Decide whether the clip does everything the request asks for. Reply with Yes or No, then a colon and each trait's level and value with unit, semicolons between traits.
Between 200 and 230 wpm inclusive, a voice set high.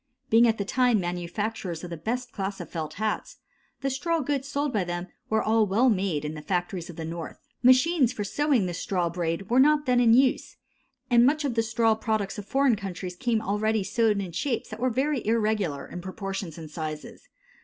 Yes: fast, 205 wpm; high, 215 Hz